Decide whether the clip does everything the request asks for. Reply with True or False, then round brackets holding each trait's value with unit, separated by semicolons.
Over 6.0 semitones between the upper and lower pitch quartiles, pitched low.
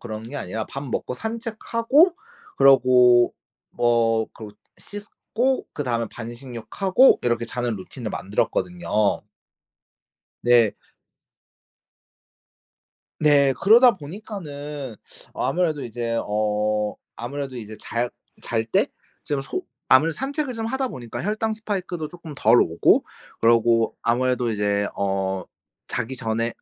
True (7.8 semitones; 125 Hz)